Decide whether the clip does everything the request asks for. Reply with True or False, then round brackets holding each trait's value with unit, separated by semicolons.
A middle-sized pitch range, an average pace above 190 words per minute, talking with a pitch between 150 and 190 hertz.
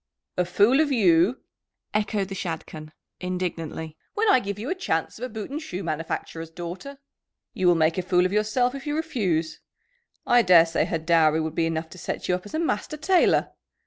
False (6.8 semitones; 200 wpm; 185 Hz)